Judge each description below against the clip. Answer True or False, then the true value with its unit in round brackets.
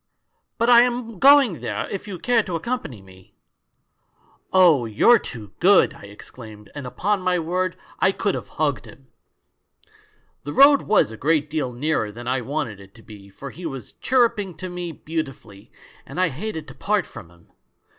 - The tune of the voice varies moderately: False (8.8 semitones)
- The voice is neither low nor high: True (160 Hz)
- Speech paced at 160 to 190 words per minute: True (185 wpm)